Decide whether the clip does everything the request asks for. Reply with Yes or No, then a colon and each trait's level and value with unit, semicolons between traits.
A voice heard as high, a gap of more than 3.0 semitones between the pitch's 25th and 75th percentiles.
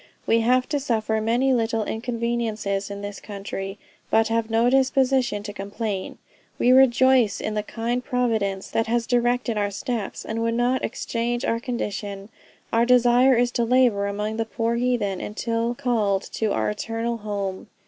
No: high, 230 Hz; average, 2.7 semitones